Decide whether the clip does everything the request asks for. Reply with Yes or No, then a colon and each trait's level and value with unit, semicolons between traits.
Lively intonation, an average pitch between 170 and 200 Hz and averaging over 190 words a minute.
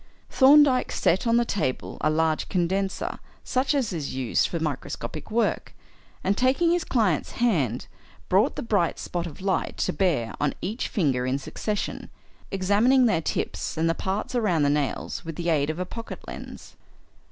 No: wide, 6.7 semitones; medium, 185 Hz; average, 170 wpm